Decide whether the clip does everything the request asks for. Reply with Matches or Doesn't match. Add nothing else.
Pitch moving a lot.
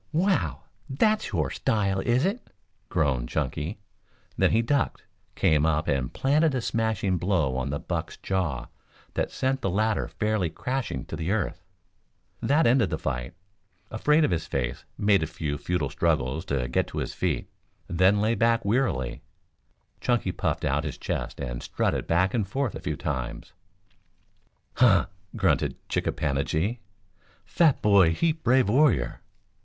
Matches